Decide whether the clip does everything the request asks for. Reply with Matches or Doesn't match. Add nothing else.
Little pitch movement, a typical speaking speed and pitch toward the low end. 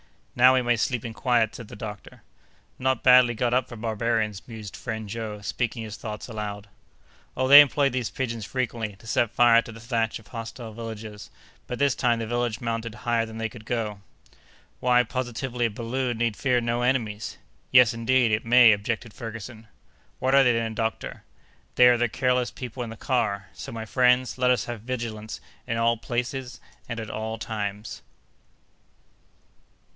Matches